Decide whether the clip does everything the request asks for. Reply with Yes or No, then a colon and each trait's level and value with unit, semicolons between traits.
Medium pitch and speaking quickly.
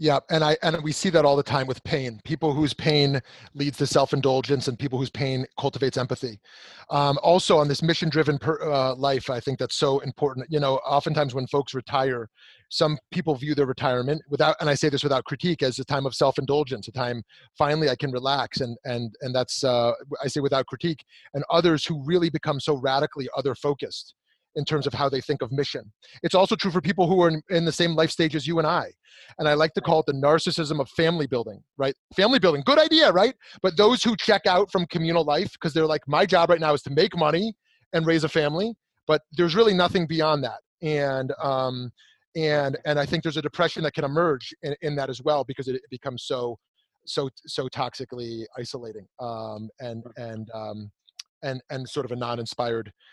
Yes: medium, 145 Hz; fast, 215 wpm